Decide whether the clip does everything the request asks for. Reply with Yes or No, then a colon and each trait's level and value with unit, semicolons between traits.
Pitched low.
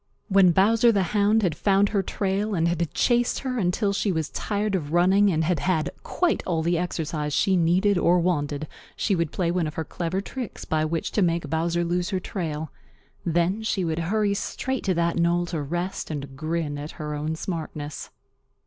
No: medium, 175 Hz